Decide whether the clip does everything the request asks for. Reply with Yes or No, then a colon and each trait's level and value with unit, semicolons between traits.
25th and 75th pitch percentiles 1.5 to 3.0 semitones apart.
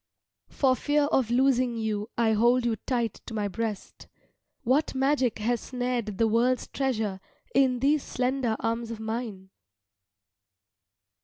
Yes: average, 2.7 semitones